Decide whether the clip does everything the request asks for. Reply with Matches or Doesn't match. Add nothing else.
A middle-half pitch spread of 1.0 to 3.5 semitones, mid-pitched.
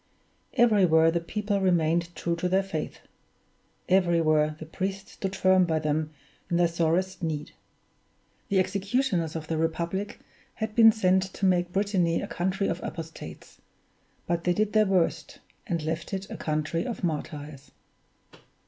Matches